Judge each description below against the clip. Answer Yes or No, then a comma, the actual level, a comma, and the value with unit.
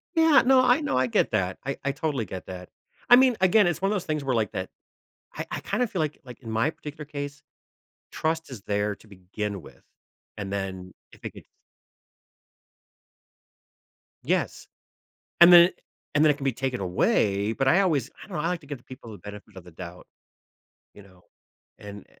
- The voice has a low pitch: Yes, low, 130 Hz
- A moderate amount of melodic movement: No, wide, 8.1 semitones